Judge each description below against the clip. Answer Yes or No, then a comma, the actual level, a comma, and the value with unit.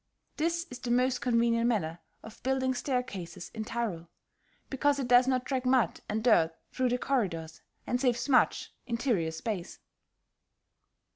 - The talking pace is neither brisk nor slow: Yes, average, 145 wpm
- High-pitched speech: Yes, high, 245 Hz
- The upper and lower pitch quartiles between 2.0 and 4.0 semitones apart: Yes, average, 3.6 semitones